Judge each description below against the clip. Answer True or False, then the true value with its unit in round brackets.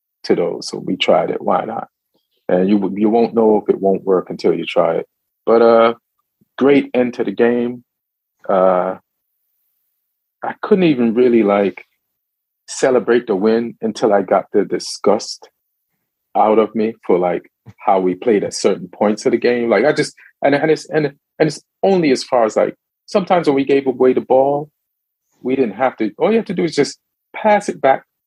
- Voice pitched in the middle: False (120 Hz)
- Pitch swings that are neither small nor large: True (4.5 semitones)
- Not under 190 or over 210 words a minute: True (195 wpm)